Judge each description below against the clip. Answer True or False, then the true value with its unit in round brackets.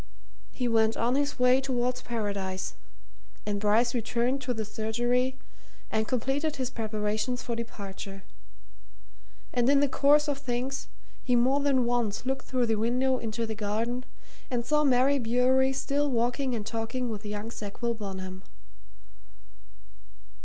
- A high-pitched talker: True (240 Hz)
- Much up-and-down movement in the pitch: False (3.1 semitones)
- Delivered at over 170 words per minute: False (140 wpm)